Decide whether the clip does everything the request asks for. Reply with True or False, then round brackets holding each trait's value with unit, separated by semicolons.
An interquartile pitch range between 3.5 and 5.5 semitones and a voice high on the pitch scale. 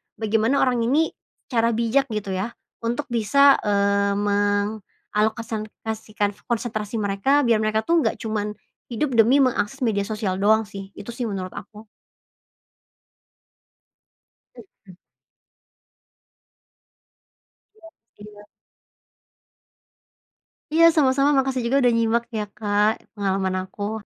False (2.8 semitones; 220 Hz)